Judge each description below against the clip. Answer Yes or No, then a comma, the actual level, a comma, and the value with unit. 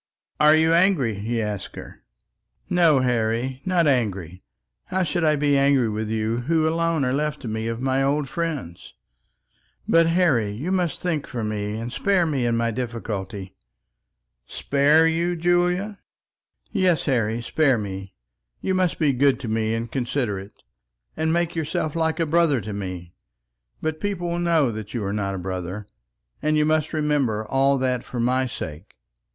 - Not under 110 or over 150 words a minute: No, average, 165 wpm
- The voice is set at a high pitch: No, low, 135 Hz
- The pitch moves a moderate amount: No, wide, 6.5 semitones